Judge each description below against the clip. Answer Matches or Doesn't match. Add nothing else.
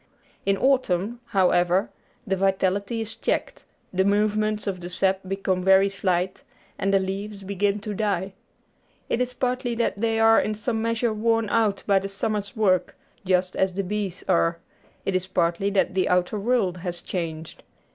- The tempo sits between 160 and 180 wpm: Matches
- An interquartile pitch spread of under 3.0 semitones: Matches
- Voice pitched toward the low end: Doesn't match